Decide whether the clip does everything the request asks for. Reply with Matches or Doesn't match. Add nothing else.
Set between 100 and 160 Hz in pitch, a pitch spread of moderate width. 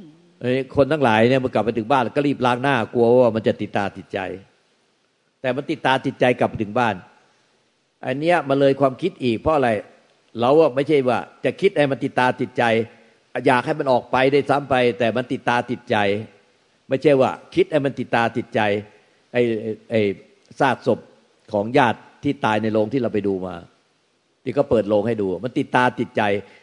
Matches